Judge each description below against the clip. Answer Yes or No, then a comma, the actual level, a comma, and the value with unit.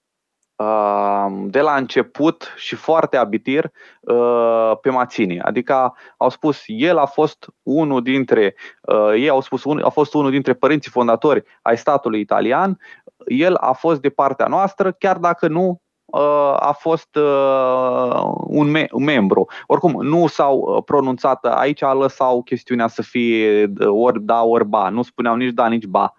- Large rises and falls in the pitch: No, average, 4.2 semitones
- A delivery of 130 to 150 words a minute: Yes, average, 135 wpm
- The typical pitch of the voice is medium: No, low, 130 Hz